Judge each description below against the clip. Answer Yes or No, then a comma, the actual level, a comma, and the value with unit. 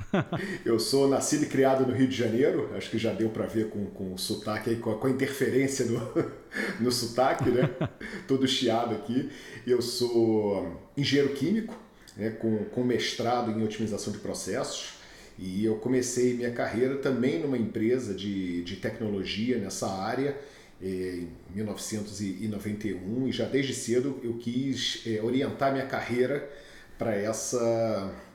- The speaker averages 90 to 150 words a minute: Yes, average, 145 wpm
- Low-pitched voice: Yes, low, 115 Hz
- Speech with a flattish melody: No, average, 3.3 semitones